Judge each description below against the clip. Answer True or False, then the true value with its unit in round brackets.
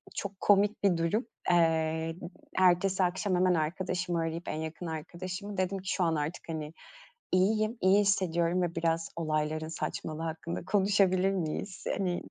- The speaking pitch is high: False (175 Hz)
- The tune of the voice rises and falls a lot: False (2.8 semitones)